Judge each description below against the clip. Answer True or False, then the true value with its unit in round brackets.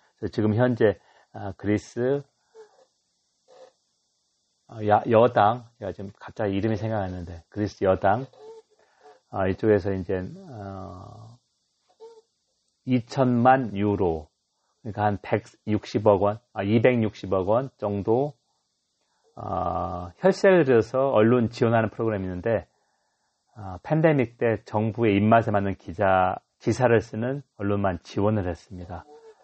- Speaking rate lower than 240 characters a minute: True (205 characters per minute)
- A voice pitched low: True (110 Hz)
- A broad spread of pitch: False (4.0 semitones)